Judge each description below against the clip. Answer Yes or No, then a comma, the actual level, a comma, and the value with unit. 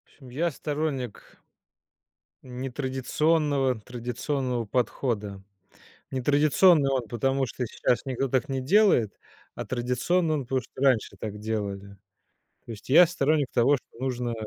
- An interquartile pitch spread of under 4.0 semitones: Yes, average, 3.2 semitones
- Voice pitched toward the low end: Yes, low, 130 Hz